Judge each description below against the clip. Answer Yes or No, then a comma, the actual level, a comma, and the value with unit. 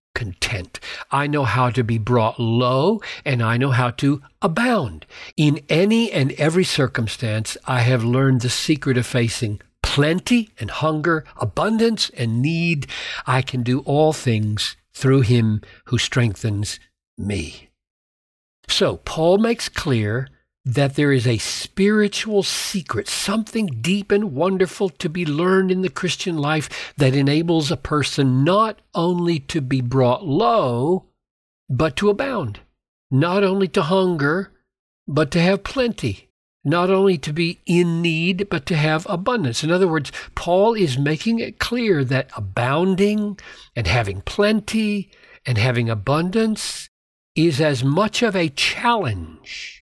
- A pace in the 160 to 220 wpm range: No, average, 140 wpm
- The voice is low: No, medium, 155 Hz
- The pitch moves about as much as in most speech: No, wide, 6.8 semitones